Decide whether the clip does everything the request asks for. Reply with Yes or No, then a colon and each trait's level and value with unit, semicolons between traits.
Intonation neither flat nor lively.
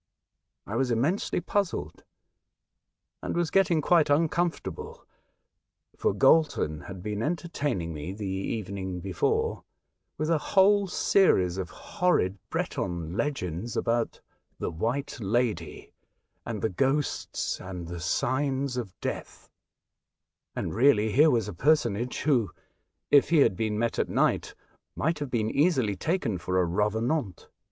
No: wide, 8.1 semitones